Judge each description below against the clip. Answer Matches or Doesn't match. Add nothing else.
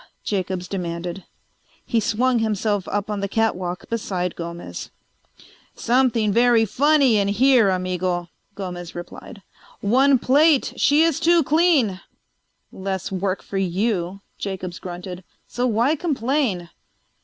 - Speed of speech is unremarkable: Doesn't match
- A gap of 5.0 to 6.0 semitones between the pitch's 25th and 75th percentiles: Matches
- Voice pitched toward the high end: Matches